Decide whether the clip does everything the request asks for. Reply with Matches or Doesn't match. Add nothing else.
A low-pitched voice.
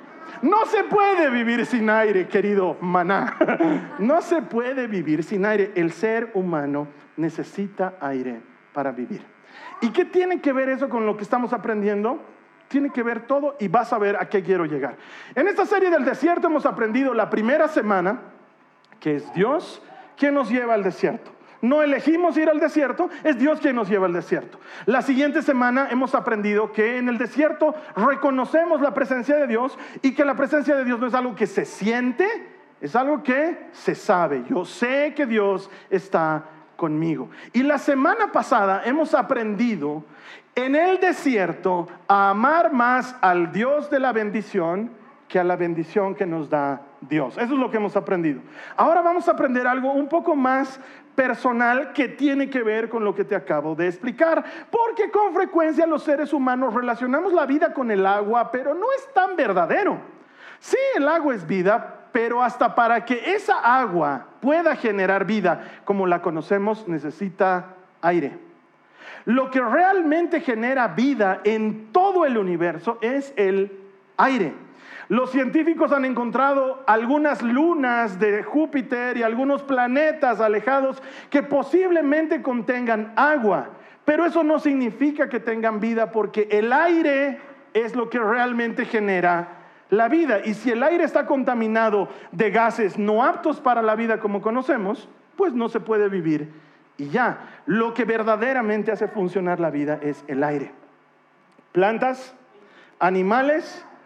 Doesn't match